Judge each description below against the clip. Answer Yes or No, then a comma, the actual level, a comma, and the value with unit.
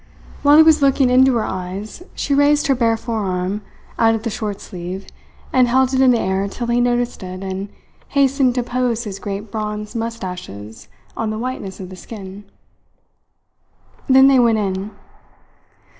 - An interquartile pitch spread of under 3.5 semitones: No, average, 4.6 semitones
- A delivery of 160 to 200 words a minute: Yes, average, 170 wpm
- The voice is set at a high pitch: Yes, high, 225 Hz